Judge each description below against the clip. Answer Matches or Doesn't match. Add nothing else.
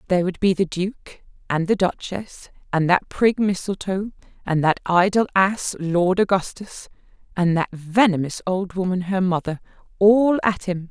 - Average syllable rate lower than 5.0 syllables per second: Matches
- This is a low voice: Doesn't match